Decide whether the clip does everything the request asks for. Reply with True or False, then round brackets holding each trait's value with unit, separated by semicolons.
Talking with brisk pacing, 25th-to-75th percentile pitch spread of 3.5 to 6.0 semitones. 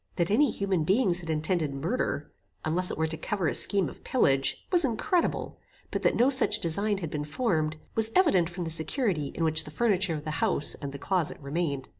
True (210 wpm; 5.3 semitones)